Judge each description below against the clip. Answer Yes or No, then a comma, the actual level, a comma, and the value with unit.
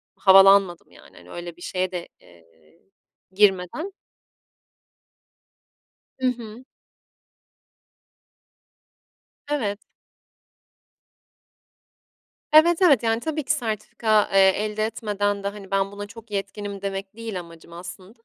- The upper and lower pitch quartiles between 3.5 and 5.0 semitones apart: No, average, 3.1 semitones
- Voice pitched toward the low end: No, high, 200 Hz